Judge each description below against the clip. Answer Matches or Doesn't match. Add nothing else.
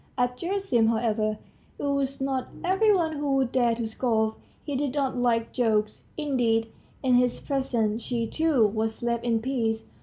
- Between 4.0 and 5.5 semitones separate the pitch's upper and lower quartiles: Doesn't match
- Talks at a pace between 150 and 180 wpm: Matches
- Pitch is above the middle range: Matches